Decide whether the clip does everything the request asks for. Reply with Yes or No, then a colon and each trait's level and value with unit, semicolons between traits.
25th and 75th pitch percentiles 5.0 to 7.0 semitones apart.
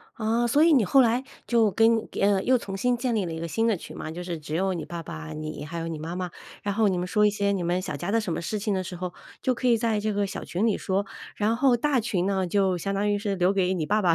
No: average, 4.2 semitones